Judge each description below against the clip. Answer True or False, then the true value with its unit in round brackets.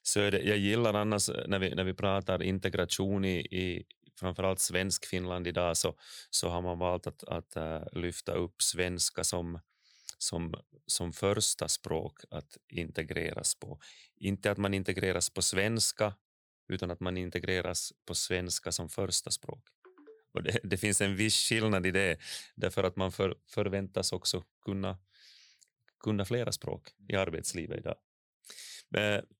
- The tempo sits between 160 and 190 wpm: False (150 wpm)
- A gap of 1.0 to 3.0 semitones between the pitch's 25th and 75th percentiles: True (2.6 semitones)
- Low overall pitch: True (95 Hz)